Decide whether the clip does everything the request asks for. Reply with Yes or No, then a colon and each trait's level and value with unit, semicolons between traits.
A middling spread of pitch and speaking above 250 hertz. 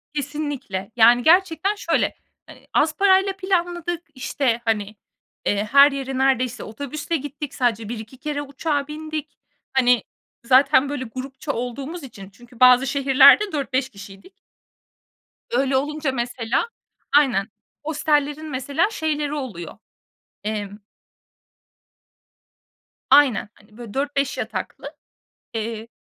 Yes: average, 4.0 semitones; very high, 270 Hz